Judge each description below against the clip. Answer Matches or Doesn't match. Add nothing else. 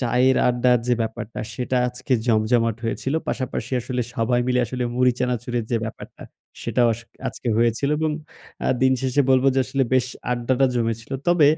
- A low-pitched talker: Matches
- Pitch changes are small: Matches